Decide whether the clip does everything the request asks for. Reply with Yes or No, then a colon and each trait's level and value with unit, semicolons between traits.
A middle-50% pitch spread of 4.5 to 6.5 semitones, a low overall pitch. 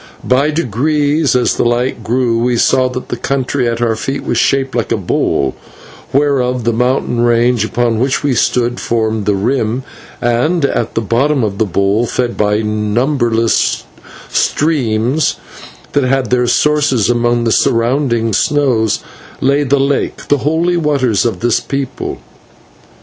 No: average, 3.2 semitones; low, 125 Hz